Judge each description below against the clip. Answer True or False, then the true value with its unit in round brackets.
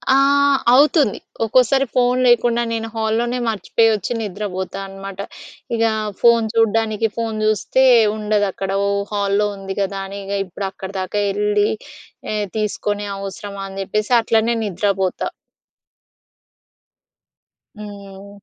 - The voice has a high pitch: True (210 Hz)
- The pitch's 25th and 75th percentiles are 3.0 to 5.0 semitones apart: False (2.5 semitones)